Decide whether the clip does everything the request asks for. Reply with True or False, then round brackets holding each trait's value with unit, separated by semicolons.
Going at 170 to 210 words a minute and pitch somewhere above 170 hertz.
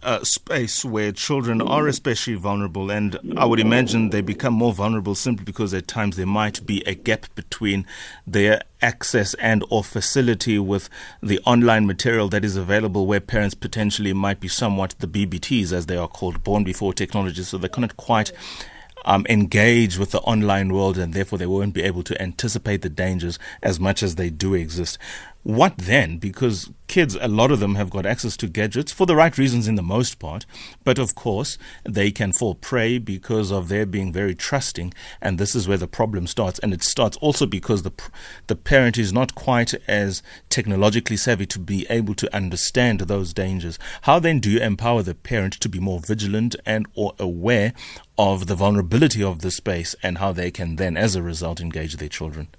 False (195 wpm; 100 Hz)